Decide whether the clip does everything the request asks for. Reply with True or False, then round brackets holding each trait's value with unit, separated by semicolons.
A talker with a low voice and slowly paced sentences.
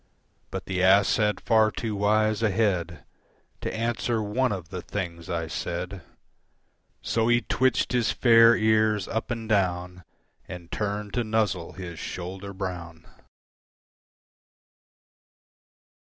True (100 Hz; 125 wpm)